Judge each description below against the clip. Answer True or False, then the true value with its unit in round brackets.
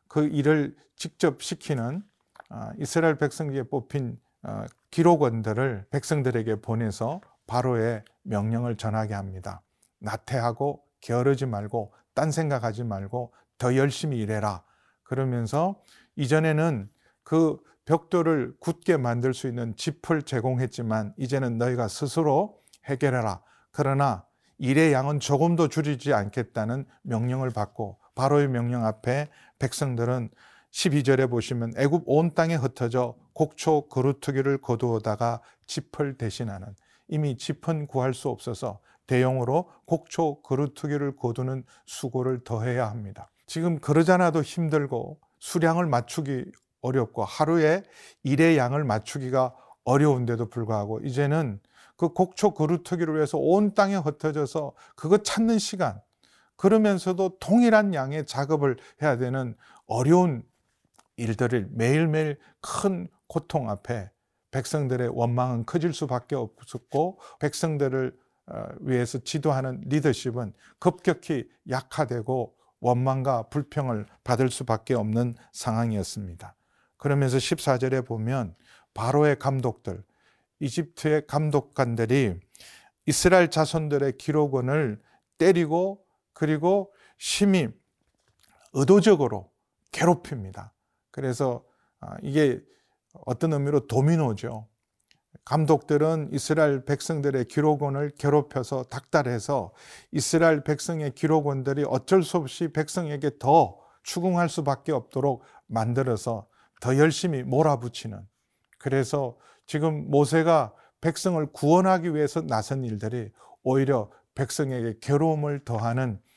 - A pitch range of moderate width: True (4.6 semitones)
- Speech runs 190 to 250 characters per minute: False (275 characters per minute)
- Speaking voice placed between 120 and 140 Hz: True (135 Hz)